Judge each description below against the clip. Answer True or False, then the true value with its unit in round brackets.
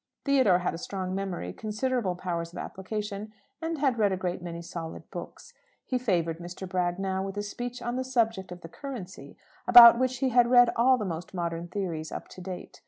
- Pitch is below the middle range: False (195 Hz)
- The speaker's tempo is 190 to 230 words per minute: True (205 wpm)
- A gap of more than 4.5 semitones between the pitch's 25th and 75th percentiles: True (5.4 semitones)